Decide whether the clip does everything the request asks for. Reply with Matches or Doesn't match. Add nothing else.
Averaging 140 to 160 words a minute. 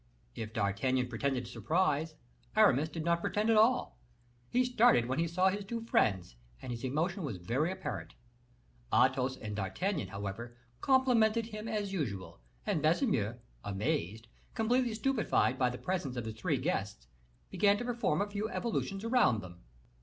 Matches